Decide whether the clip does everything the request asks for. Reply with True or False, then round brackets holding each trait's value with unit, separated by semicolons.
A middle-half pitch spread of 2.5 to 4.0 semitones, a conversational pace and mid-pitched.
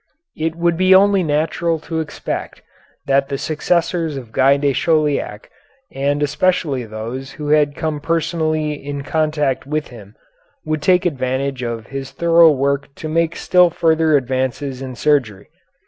True (3.2 semitones; 145 wpm; 150 Hz)